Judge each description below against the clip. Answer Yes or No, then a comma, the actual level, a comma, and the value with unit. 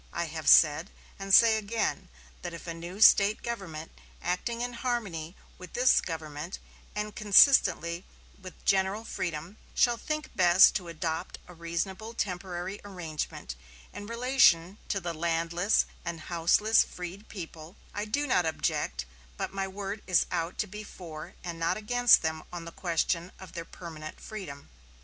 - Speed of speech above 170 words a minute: No, average, 155 wpm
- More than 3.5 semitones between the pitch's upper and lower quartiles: Yes, average, 4.0 semitones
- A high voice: No, medium, 180 Hz